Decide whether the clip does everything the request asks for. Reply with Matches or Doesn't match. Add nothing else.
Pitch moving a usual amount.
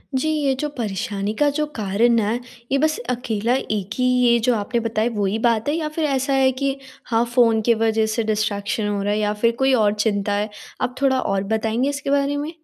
Matches